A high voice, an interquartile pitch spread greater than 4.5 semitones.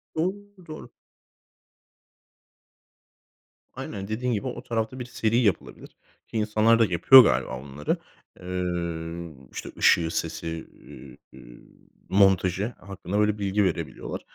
No: low, 100 Hz; average, 4.9 semitones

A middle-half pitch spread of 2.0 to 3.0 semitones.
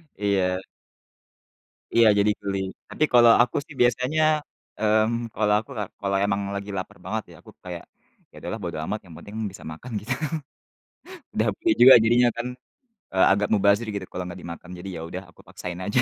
No: average, 3.9 semitones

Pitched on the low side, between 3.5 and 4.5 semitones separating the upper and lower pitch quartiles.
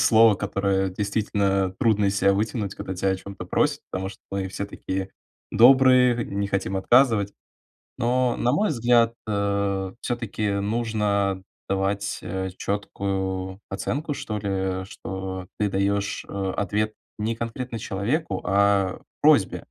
No: low, 100 Hz; narrow, 2.6 semitones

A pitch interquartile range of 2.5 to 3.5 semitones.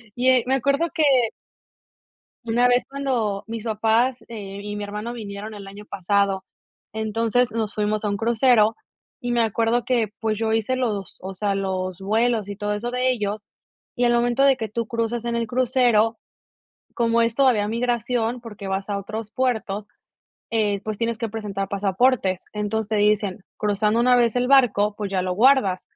Yes: average, 2.8 semitones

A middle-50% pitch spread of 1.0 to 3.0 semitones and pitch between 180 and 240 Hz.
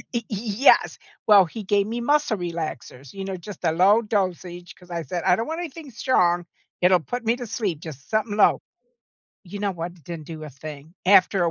No: average, 4.2 semitones; medium, 185 Hz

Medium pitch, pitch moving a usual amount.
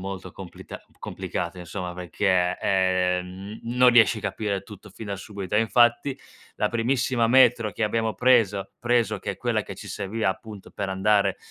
No: low, 105 Hz; average, 3.4 semitones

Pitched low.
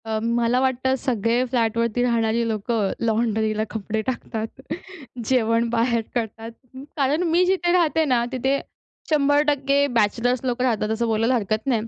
No: high, 235 Hz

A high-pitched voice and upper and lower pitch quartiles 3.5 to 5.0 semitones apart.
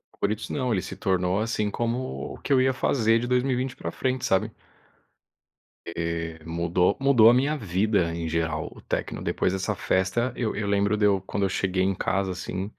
No: low, 100 Hz; average, 4.7 semitones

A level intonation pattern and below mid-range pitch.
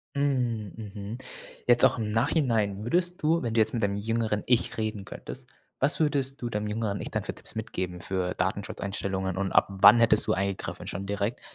No: average, 3.5 semitones; low, 110 Hz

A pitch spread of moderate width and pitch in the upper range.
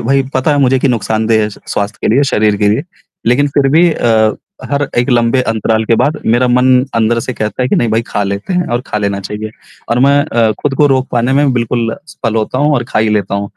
No: average, 3.7 semitones; low, 120 Hz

